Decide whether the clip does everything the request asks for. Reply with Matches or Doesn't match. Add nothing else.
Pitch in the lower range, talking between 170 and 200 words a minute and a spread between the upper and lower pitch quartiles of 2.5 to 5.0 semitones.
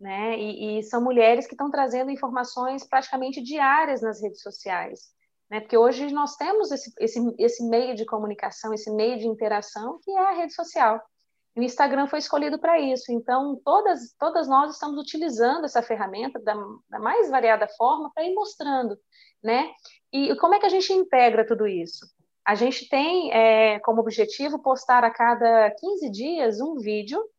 Doesn't match